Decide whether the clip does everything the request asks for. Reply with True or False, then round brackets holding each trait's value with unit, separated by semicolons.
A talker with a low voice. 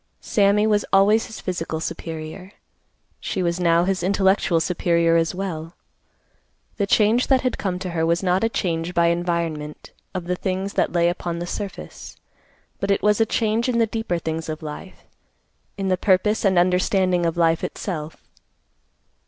False (180 Hz)